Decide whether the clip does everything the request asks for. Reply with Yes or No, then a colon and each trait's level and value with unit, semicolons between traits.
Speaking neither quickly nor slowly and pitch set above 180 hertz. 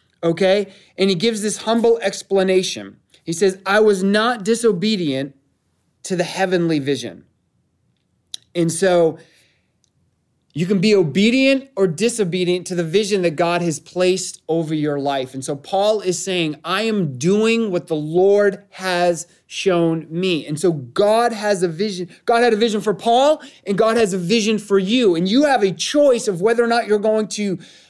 Yes: average, 170 wpm; high, 190 Hz